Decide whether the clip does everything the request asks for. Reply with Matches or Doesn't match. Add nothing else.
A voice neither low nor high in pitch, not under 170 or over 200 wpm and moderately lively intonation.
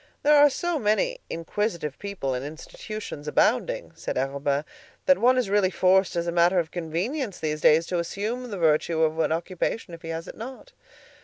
Doesn't match